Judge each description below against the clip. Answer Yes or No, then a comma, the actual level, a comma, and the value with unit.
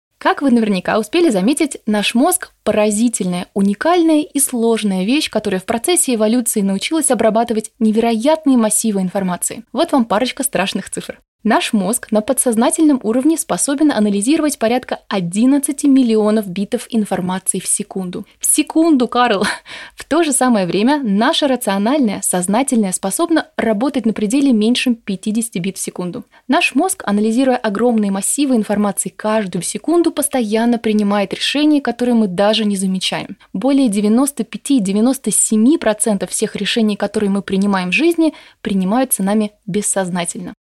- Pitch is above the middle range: Yes, high, 225 Hz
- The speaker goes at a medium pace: Yes, average, 130 wpm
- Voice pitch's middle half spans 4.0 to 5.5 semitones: Yes, average, 4.8 semitones